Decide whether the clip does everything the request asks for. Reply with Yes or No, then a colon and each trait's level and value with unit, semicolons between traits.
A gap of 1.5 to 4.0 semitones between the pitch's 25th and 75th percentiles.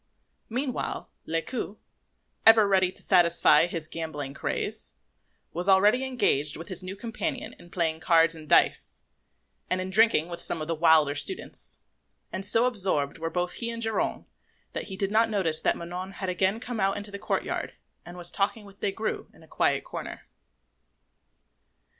No: average, 4.6 semitones